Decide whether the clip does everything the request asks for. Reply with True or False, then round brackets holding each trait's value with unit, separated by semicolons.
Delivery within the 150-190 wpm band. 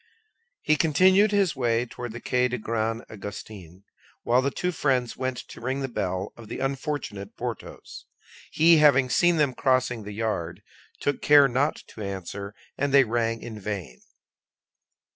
True (160 wpm)